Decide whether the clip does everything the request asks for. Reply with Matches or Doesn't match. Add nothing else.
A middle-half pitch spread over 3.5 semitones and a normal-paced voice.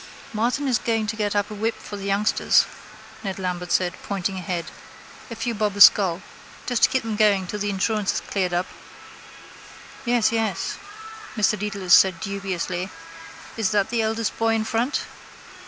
Doesn't match